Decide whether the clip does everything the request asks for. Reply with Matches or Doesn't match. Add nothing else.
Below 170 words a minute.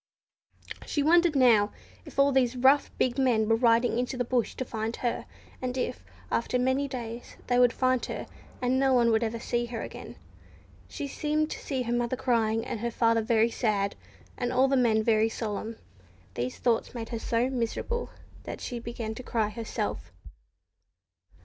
Doesn't match